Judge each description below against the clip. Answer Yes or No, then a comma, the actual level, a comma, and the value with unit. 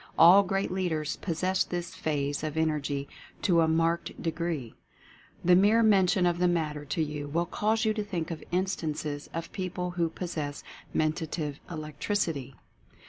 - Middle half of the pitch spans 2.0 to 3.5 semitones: Yes, average, 3.1 semitones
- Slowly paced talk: No, average, 160 wpm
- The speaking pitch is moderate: Yes, medium, 165 Hz